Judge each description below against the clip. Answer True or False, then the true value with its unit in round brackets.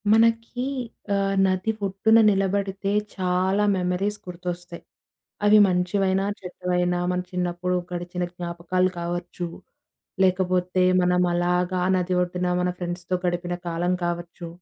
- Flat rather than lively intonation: True (1.3 semitones)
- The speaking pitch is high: False (180 Hz)